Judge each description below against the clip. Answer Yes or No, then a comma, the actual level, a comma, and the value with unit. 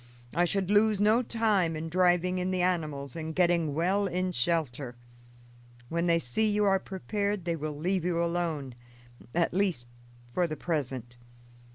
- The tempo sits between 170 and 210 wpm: No, average, 160 wpm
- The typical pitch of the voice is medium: Yes, medium, 175 Hz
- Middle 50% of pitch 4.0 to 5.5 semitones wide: No, average, 3.3 semitones